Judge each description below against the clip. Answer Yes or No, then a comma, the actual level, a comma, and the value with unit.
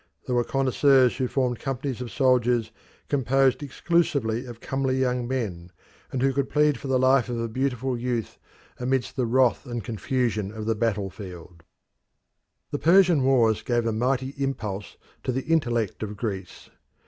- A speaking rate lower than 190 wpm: Yes, average, 160 wpm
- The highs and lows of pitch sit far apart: No, average, 2.9 semitones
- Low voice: Yes, low, 125 Hz